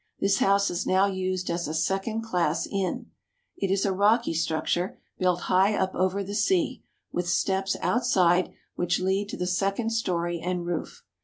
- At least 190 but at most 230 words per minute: No, average, 170 wpm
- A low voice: No, high, 190 Hz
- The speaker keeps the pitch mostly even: Yes, narrow, 2.1 semitones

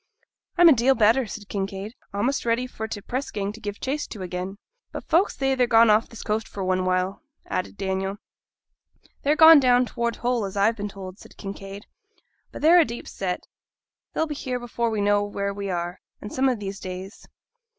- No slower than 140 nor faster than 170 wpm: No, average, 200 wpm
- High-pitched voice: Yes, high, 210 Hz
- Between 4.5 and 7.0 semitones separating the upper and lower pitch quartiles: No, average, 4.1 semitones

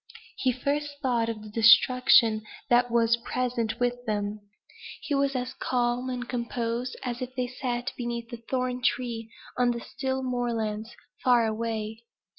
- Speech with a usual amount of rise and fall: No, narrow, 1.7 semitones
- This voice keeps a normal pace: Yes, average, 150 wpm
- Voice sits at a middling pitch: No, high, 240 Hz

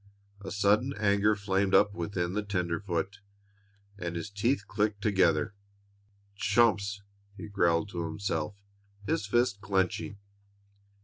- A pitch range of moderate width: No, narrow, 2.3 semitones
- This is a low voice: Yes, low, 100 Hz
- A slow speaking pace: Yes, slow, 115 wpm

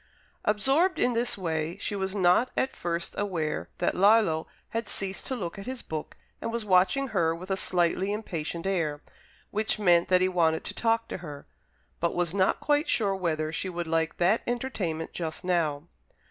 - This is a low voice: No, medium, 185 Hz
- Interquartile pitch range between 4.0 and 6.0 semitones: Yes, average, 4.4 semitones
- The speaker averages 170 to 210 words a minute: Yes, average, 185 wpm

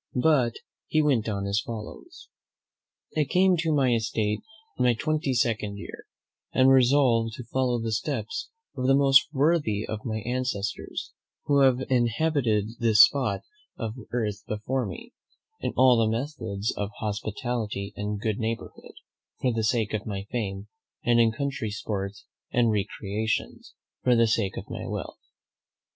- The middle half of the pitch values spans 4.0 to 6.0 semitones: No, average, 3.6 semitones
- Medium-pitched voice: No, low, 115 Hz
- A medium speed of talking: Yes, average, 150 wpm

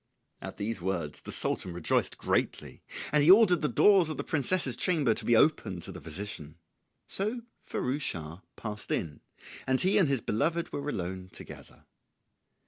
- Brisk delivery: No, average, 170 wpm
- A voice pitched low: Yes, low, 120 Hz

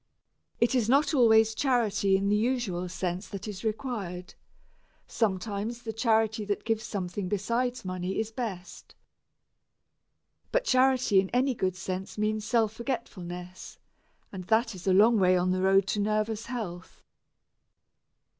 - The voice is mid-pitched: No, high, 210 Hz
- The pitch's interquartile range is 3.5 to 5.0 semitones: Yes, average, 3.8 semitones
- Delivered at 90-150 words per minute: Yes, average, 140 wpm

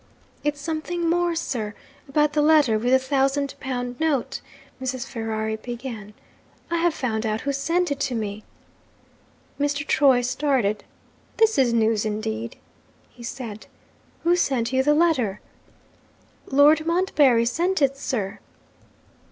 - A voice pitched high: Yes, very high, 265 Hz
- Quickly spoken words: No, slow, 135 wpm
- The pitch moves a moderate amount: Yes, average, 4.8 semitones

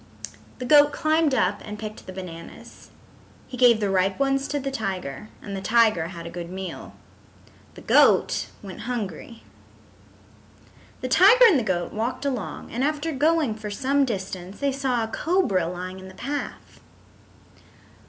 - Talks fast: No, average, 160 wpm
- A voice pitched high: Yes, high, 225 Hz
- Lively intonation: Yes, wide, 6.6 semitones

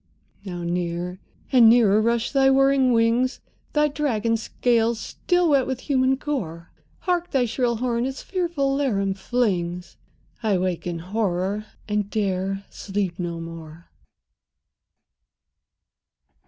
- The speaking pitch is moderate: No, high, 225 Hz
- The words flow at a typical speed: No, slow, 120 wpm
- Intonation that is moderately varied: No, wide, 6.1 semitones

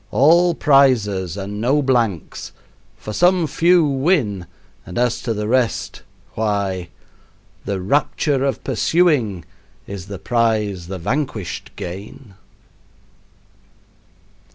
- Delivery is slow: Yes, slow, 105 wpm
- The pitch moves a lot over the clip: Yes, wide, 6.0 semitones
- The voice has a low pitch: Yes, low, 115 Hz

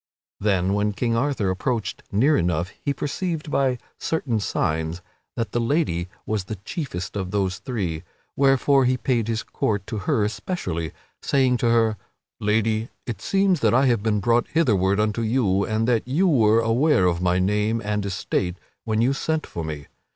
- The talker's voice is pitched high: No, low, 110 Hz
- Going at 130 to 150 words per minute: No, average, 175 wpm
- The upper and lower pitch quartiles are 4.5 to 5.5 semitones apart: Yes, average, 4.9 semitones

